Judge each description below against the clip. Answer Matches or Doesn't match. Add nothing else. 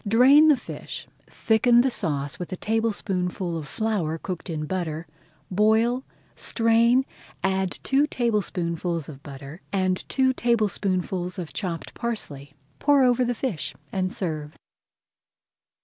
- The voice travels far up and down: Matches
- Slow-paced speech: Matches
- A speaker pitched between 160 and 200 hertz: Matches